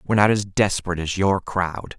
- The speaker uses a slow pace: No, fast, 210 wpm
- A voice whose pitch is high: No, very low, 95 Hz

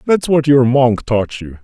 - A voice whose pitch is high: No, low, 130 Hz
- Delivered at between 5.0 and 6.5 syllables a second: No, 4.1 syllables/s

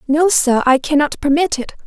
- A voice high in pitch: Yes, very high, 295 Hz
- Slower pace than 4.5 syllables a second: No, 5.4 syllables/s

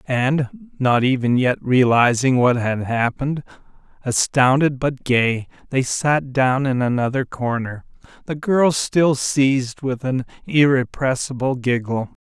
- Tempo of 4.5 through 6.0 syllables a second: No, 4.0 syllables/s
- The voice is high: No, low, 130 Hz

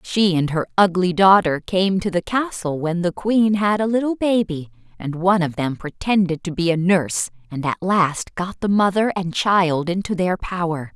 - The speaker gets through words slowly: No, average, 195 wpm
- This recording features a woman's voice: Yes, female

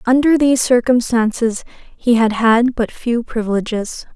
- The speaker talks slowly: Yes, slow, 130 wpm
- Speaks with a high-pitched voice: Yes, high, 235 Hz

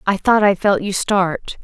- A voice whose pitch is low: No, high, 195 Hz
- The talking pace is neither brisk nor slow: No, fast, 220 wpm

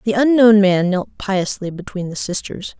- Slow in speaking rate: No, average, 170 wpm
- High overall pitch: Yes, high, 195 Hz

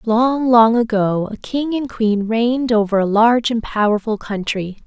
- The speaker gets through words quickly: No, average, 175 wpm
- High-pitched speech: Yes, high, 225 Hz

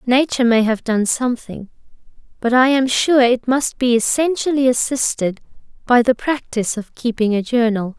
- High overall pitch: Yes, high, 245 Hz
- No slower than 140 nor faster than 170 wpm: Yes, average, 160 wpm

